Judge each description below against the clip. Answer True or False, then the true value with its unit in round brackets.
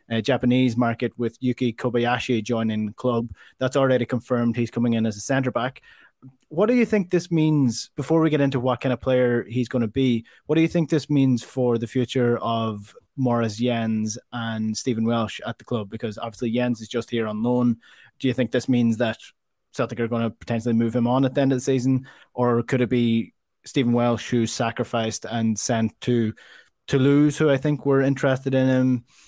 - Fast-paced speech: True (210 wpm)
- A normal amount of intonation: False (2.2 semitones)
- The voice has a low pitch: True (125 Hz)